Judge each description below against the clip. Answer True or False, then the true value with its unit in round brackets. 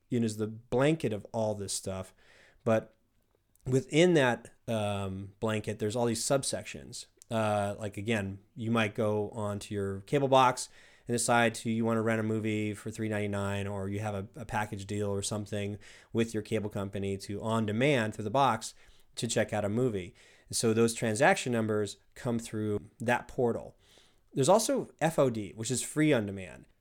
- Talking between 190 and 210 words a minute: False (180 wpm)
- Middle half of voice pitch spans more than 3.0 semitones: False (2.6 semitones)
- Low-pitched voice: True (110 Hz)